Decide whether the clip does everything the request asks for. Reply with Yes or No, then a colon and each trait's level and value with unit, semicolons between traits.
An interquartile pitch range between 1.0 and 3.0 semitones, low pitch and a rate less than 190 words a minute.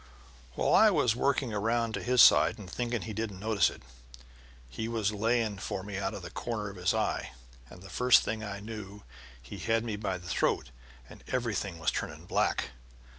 No: average, 2.7 semitones; low, 105 Hz; average, 195 wpm